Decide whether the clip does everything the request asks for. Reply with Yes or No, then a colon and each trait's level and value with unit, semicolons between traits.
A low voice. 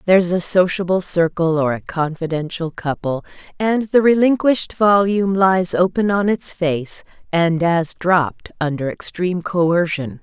No: medium, 175 Hz